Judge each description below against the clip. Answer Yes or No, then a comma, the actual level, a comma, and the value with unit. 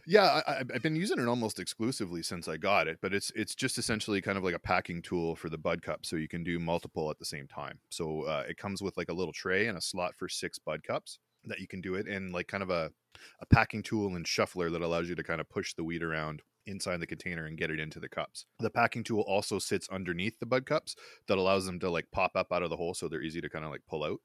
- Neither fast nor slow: No, fast, 285 wpm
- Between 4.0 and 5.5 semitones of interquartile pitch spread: Yes, average, 4.4 semitones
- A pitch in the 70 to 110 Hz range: Yes, very low, 90 Hz